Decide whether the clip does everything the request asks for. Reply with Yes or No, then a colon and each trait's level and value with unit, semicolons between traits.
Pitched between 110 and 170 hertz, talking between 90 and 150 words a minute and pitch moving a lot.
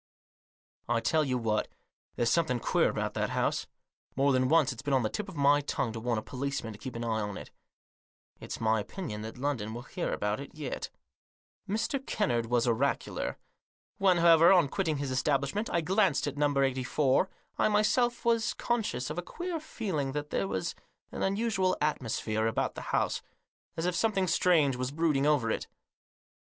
No: medium, 140 Hz; average, 185 wpm; wide, 6.6 semitones